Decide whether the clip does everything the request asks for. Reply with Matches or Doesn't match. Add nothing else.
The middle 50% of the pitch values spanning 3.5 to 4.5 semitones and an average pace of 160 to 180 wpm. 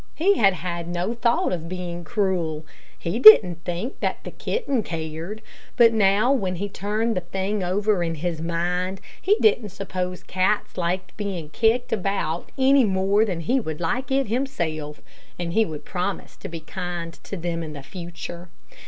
Matches